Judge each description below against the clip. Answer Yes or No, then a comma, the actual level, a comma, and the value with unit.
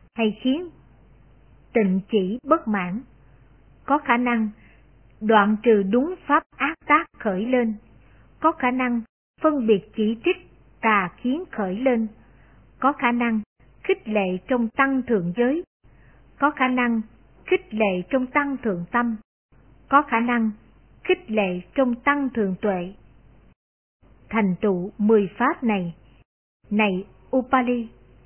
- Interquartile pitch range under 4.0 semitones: No, average, 4.3 semitones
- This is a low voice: No, high, 230 Hz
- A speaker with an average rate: No, slow, 130 wpm